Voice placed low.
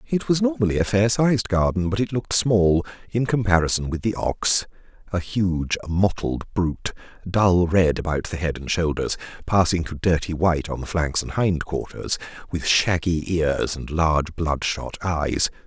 Yes: very low, 90 Hz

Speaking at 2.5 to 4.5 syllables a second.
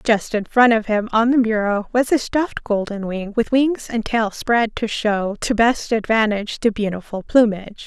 No: 4.7 syllables/s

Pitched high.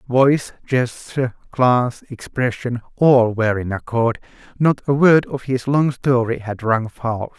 No: low, 125 Hz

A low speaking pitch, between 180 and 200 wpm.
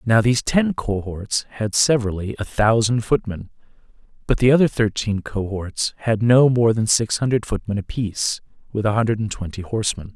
No: low, 110 Hz; average, 165 wpm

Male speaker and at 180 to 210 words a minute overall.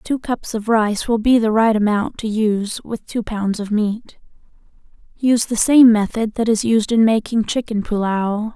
No: female; average, 190 wpm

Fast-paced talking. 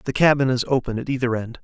Yes: fast, 260 wpm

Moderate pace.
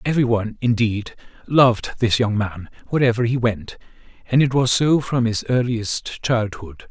Yes: average, 155 wpm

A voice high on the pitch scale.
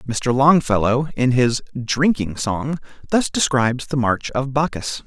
No: low, 130 Hz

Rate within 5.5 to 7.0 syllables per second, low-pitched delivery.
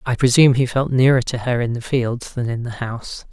Yes: 5.7 syllables/s; low, 125 Hz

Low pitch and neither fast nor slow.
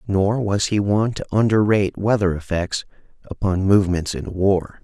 Yes: low, 100 Hz; average, 150 wpm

